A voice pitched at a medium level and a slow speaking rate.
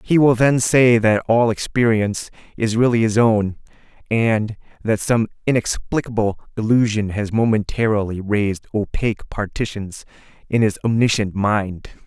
No: low, 110 Hz; slow, 125 wpm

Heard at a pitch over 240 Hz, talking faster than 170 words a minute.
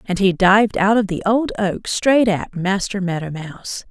No: high, 195 Hz; average, 200 wpm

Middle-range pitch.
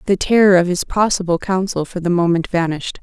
Yes: medium, 180 Hz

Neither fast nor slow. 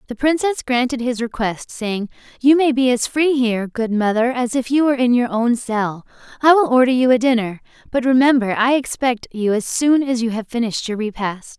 No: fast, 210 wpm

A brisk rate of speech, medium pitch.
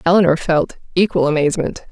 No: slow, 125 wpm; medium, 165 Hz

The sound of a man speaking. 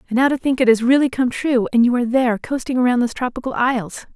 No: female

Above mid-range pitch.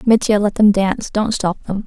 Yes: high, 205 Hz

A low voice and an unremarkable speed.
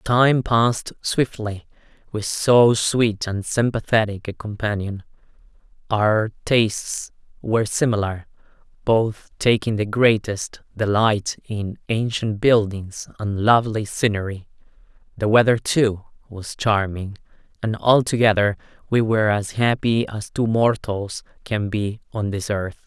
No: low, 110 Hz; slow, 115 wpm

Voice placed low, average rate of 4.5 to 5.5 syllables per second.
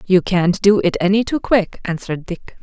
No: high, 190 Hz; 4.9 syllables/s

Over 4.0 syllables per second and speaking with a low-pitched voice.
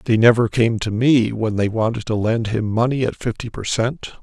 Yes: 5.0 syllables/s; low, 115 Hz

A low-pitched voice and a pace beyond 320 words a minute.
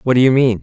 Yes: low, 120 Hz; fast, 385 wpm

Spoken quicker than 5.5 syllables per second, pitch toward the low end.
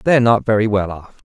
Yes: 6.5 syllables/s; low, 110 Hz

